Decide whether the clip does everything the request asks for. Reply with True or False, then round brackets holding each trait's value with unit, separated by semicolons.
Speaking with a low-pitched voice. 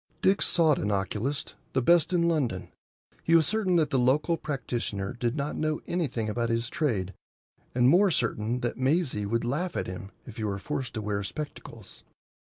True (130 Hz)